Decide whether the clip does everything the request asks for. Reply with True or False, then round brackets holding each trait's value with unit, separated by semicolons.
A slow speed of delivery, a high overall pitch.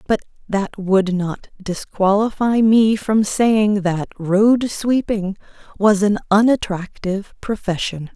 True (110 wpm; 205 Hz)